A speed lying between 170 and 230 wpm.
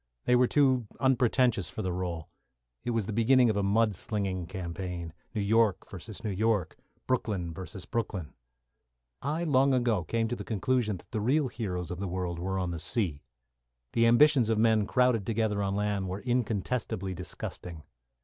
Yes: average, 175 wpm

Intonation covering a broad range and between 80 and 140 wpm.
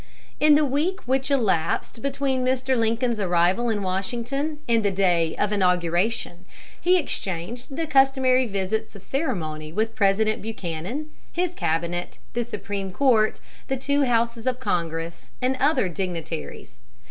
Yes: wide, 6.5 semitones; slow, 135 wpm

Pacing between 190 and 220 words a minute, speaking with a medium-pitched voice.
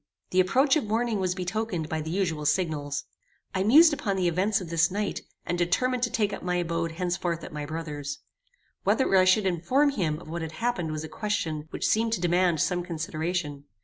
Yes: fast, 205 wpm; medium, 180 Hz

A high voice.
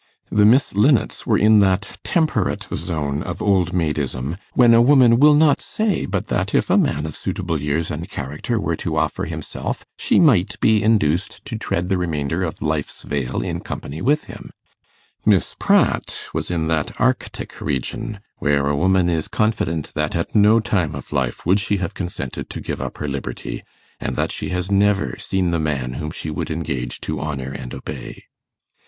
No: very low, 85 Hz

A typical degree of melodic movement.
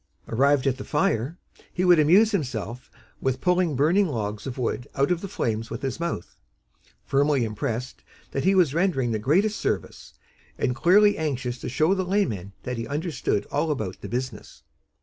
No: wide, 6.5 semitones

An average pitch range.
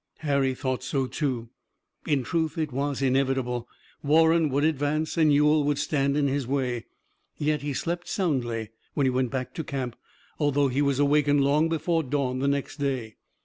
No: narrow, 2.3 semitones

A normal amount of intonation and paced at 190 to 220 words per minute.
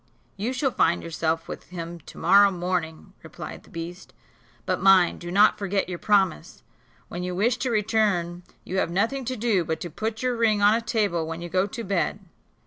Yes: average, 4.1 semitones; average, 200 wpm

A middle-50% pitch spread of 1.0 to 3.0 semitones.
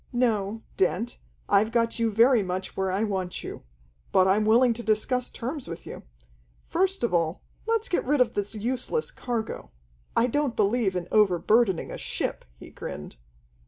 No: average, 4.2 semitones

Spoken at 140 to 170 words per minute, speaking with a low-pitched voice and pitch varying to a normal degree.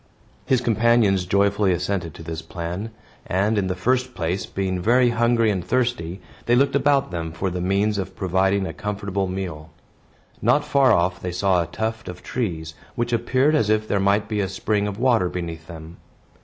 No: average, 185 wpm; low, 100 Hz; average, 4.3 semitones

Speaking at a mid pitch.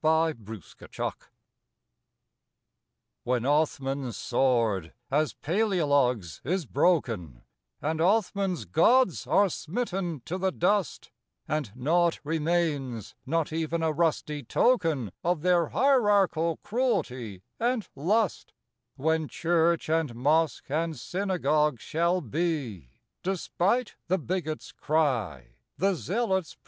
Yes: medium, 160 Hz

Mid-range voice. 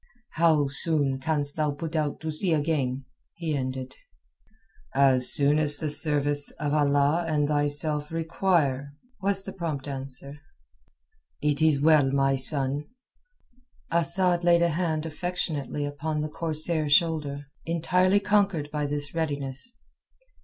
Yes: medium, 150 Hz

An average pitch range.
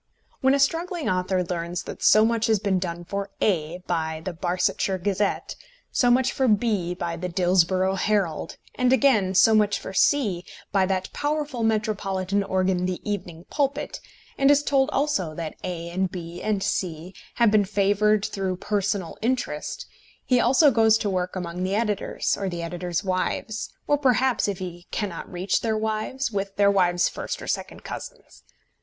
Yes: average, 3.7 semitones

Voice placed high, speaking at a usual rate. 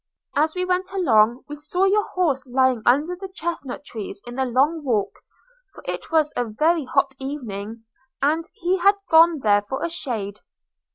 Yes: very high, 285 Hz; average, 170 wpm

